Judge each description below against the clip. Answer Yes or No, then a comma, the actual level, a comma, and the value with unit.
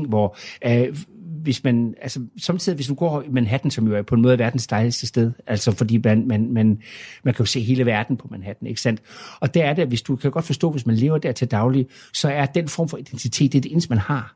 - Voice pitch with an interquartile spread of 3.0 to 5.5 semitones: Yes, average, 3.6 semitones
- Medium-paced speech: No, fast, 265 wpm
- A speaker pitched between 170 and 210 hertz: No, low, 125 Hz